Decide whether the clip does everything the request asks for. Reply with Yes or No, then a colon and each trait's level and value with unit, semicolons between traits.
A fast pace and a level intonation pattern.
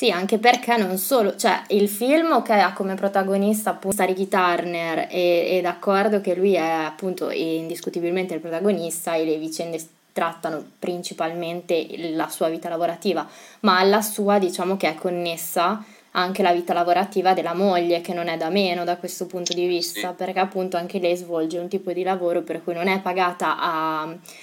Yes: fast, 175 wpm; narrow, 2.3 semitones